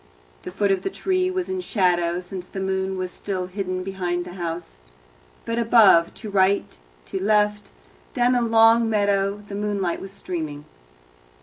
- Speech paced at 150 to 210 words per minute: Yes, average, 165 wpm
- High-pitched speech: Yes, high, 195 Hz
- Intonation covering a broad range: No, average, 3.0 semitones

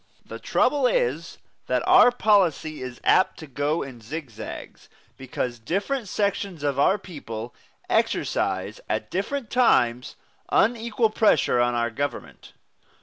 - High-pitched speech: No, medium, 160 Hz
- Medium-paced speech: No, slow, 125 wpm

